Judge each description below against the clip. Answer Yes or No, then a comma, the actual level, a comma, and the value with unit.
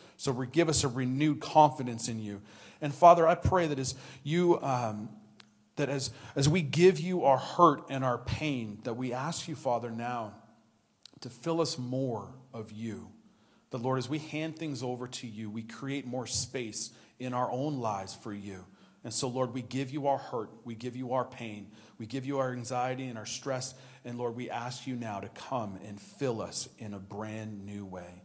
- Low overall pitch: Yes, low, 125 Hz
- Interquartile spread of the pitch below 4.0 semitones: Yes, average, 3.6 semitones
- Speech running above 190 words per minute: Yes, average, 200 wpm